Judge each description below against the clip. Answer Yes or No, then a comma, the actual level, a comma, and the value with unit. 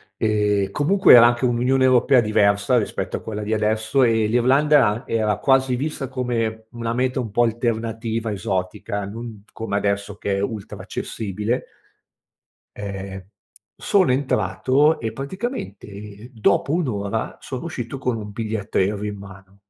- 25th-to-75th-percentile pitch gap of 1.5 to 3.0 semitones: No, average, 3.7 semitones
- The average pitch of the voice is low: Yes, low, 110 Hz